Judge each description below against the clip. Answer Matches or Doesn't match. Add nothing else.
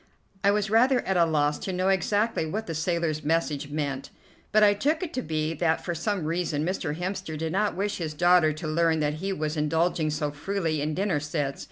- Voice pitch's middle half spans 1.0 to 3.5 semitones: Doesn't match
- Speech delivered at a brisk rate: Matches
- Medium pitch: Matches